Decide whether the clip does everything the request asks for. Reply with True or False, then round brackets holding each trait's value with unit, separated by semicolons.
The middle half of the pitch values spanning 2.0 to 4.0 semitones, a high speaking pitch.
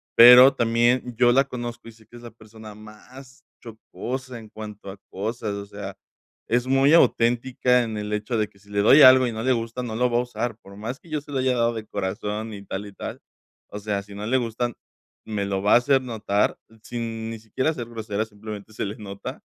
False (2.8 semitones; 115 Hz)